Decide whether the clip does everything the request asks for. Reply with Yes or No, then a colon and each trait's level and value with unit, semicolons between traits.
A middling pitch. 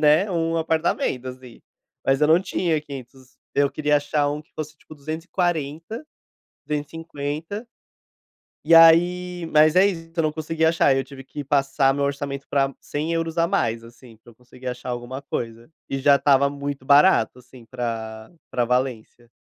Yes: medium, 145 Hz